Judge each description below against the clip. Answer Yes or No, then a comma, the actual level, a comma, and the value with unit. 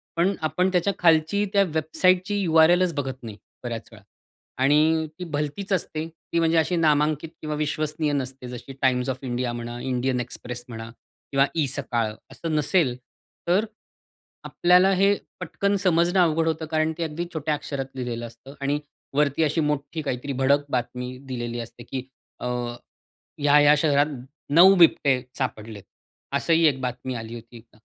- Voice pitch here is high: No, medium, 150 Hz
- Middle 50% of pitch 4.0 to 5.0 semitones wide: Yes, average, 4.5 semitones